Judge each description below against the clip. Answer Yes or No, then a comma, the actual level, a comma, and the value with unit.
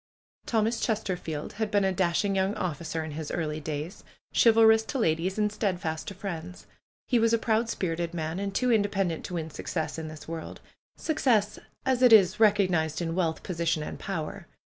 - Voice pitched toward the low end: No, medium, 185 Hz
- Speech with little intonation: No, average, 4.9 semitones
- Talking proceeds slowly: No, average, 185 wpm